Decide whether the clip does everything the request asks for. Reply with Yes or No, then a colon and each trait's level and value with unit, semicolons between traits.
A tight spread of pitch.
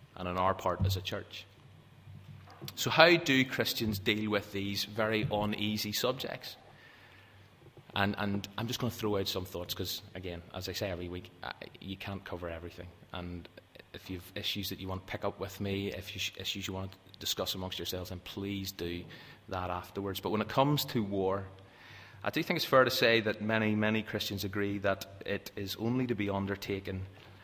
Yes: narrow, 2.2 semitones